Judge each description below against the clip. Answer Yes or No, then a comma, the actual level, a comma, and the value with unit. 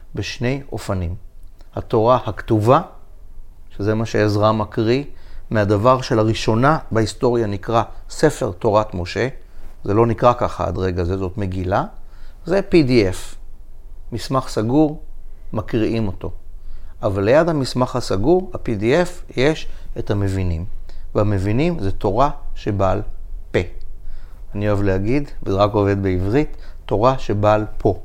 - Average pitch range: Yes, average, 4.7 semitones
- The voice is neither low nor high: No, low, 105 Hz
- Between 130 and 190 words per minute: No, average, 115 wpm